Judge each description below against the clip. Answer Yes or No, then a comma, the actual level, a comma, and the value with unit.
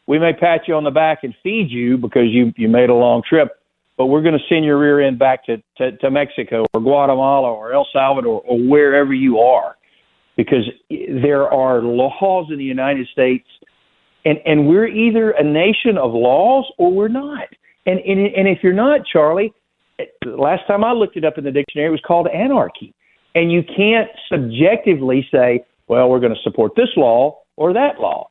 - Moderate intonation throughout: No, wide, 6.8 semitones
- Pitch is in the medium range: Yes, medium, 150 Hz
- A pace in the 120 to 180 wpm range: No, average, 200 wpm